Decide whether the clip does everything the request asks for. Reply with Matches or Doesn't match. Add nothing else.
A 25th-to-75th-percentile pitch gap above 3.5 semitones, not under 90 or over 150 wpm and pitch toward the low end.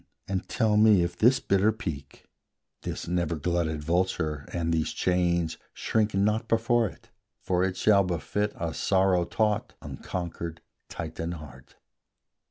Matches